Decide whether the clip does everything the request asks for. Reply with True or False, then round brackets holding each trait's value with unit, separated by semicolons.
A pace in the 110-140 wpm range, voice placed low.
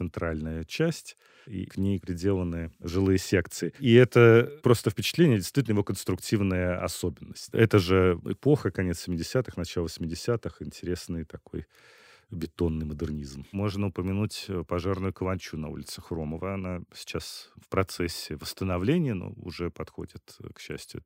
True (125 wpm; 95 Hz)